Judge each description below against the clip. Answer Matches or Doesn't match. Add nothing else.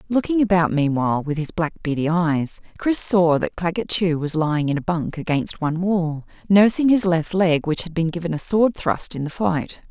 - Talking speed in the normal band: Doesn't match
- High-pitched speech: Doesn't match